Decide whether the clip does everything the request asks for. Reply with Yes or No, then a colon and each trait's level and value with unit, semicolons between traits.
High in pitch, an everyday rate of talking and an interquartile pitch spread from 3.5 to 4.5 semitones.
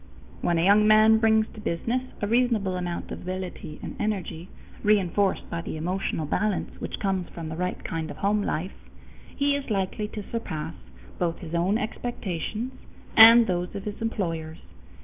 Yes: high, 195 Hz; average, 170 wpm; average, 4.0 semitones